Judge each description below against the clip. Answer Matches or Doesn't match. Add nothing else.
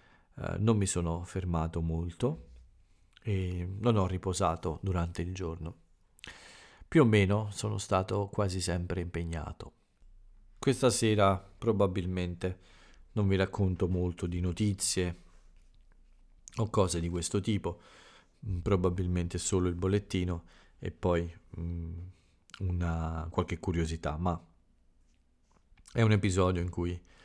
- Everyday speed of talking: Doesn't match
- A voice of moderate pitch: Doesn't match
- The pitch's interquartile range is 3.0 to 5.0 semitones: Doesn't match